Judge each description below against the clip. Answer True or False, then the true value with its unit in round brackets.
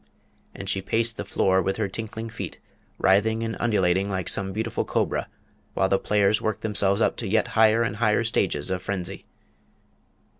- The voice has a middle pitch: False (105 Hz)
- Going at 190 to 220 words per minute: False (175 wpm)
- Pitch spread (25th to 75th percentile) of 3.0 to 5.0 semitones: False (2.6 semitones)